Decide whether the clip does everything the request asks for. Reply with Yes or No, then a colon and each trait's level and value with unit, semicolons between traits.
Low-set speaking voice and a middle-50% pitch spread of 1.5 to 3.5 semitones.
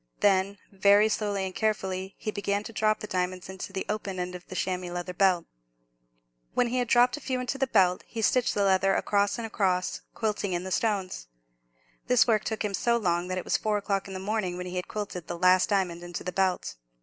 No: high, 195 Hz; average, 2.7 semitones